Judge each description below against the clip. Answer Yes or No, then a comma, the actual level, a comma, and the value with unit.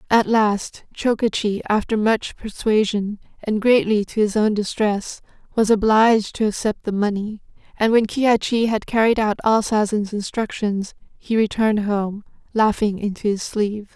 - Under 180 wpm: Yes, average, 145 wpm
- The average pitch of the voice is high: Yes, high, 215 Hz